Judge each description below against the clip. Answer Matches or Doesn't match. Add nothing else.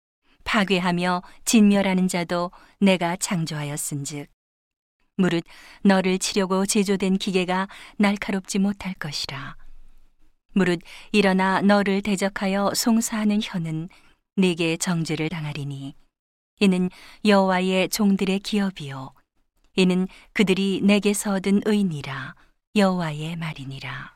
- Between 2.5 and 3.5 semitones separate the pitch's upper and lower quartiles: Matches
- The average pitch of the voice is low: Doesn't match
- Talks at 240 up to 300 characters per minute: Matches